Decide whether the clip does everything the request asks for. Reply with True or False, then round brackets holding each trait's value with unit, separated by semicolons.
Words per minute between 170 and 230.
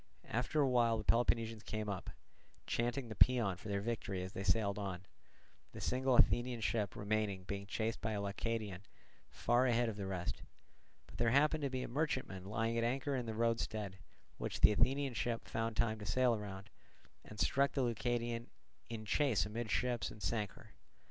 True (180 wpm)